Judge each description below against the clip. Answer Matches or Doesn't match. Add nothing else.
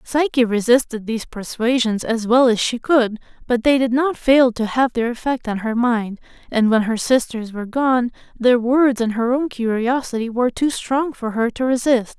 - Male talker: Doesn't match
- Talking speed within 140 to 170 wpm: Doesn't match